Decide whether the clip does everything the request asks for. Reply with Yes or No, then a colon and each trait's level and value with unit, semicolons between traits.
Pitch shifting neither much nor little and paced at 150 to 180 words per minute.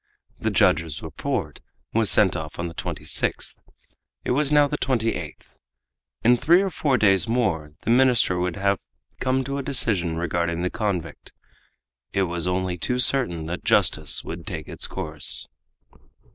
No: wide, 6.8 semitones; average, 160 wpm